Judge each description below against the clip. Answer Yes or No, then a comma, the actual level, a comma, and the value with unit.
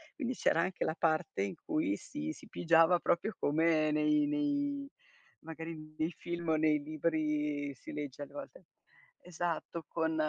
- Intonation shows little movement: No, wide, 7.5 semitones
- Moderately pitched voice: Yes, medium, 165 Hz